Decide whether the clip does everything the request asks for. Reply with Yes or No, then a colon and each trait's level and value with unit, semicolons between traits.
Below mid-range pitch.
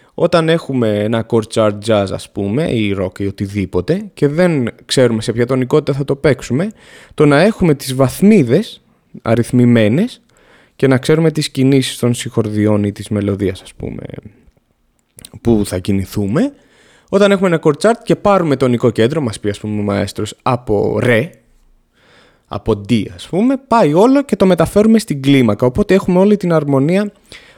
Yes: low, 130 Hz